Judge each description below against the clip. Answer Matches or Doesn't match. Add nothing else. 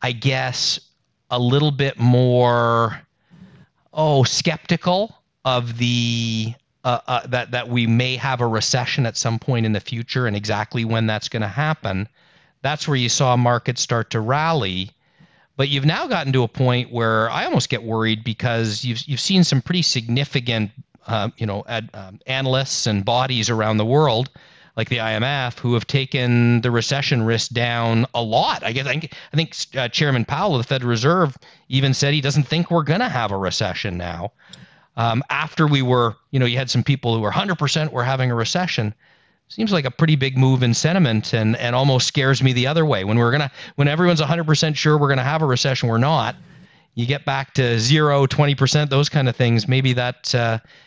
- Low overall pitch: Matches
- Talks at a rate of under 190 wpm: Doesn't match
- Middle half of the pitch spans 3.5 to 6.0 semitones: Matches